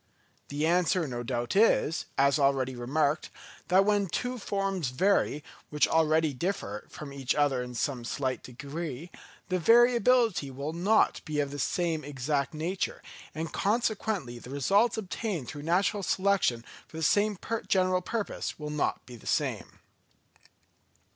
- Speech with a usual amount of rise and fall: No, wide, 6.0 semitones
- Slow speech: No, average, 145 wpm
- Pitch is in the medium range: Yes, medium, 155 Hz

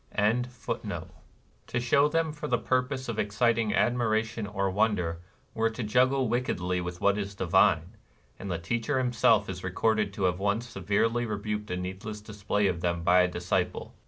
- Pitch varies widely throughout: No, average, 4.1 semitones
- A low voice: Yes, low, 105 Hz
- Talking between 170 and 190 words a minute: Yes, average, 180 wpm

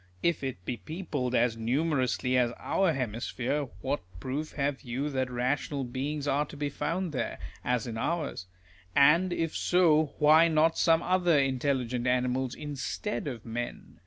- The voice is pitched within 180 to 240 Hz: No, medium, 140 Hz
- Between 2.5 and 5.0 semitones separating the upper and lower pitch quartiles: Yes, average, 3.7 semitones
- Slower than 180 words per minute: Yes, average, 155 wpm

